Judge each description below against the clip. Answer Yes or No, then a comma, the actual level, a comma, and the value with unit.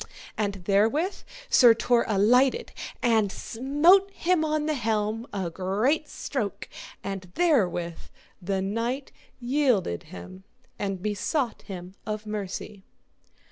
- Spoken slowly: Yes, slow, 110 wpm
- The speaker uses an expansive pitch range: Yes, wide, 5.9 semitones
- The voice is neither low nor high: No, high, 220 Hz